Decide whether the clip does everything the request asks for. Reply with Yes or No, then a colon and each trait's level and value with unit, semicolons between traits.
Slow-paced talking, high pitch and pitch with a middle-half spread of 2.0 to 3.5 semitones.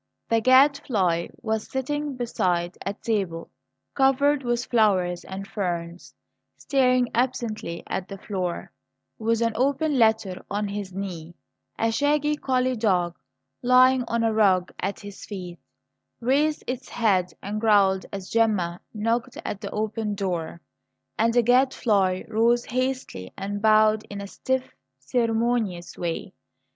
No: slow, 130 wpm; high, 220 Hz; average, 4.6 semitones